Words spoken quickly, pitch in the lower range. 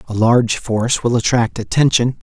No: average, 160 wpm; low, 120 Hz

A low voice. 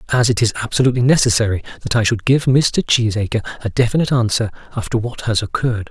Yes: low, 115 Hz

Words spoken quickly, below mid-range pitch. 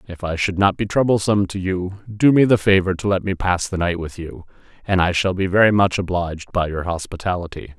Yes: fast, 230 wpm; very low, 95 Hz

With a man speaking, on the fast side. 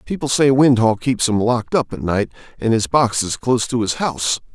Yes: male; fast, 225 wpm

